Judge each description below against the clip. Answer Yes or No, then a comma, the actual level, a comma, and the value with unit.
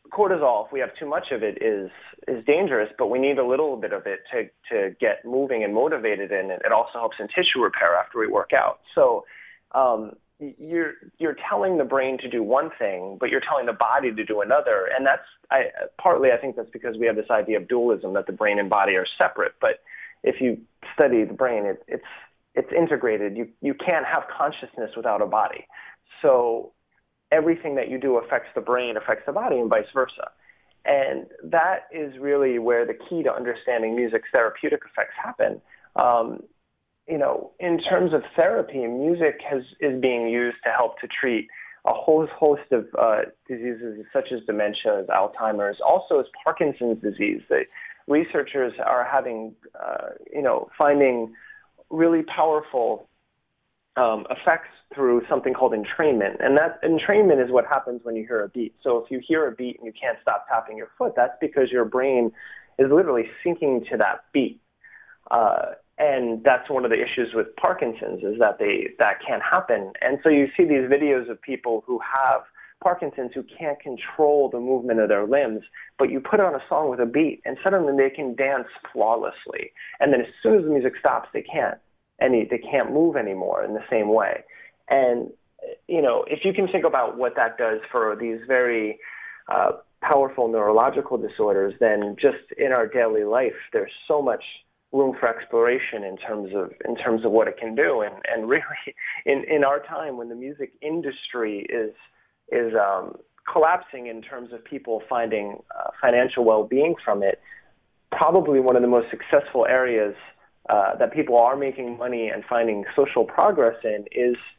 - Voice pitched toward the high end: No, medium, 140 Hz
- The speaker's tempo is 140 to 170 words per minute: No, average, 185 wpm